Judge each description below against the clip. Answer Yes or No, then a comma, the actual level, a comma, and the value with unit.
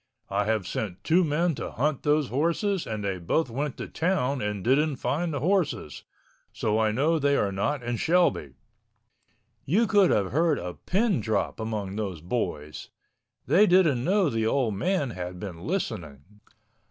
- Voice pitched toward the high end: No, low, 130 Hz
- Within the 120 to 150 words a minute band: No, average, 165 wpm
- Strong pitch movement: Yes, wide, 8.1 semitones